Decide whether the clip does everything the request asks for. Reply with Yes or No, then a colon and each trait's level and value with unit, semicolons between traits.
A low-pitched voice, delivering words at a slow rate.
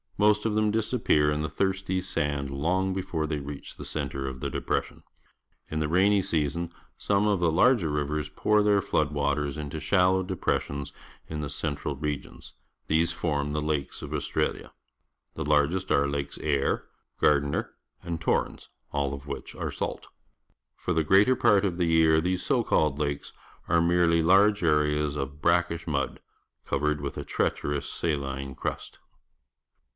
No: very low, 80 Hz; average, 160 wpm